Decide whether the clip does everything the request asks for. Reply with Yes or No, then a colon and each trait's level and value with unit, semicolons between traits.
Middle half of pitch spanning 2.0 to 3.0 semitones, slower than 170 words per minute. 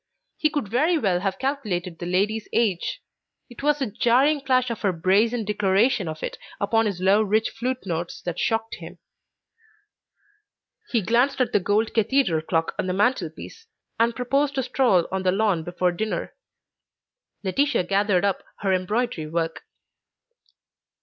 No: average, 5.3 semitones; average, 155 wpm